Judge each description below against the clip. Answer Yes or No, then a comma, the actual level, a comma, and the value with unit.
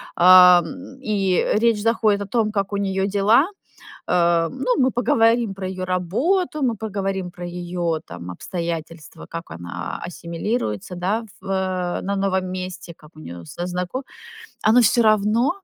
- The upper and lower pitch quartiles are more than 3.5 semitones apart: Yes, average, 4.0 semitones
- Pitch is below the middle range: No, high, 190 Hz